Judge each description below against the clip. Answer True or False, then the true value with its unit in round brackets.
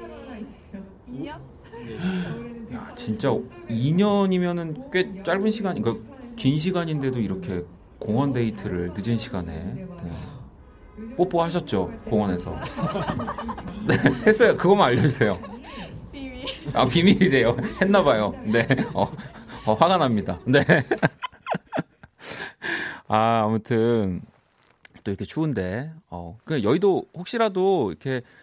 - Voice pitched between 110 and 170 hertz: True (135 Hz)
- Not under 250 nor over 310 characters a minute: False (215 characters per minute)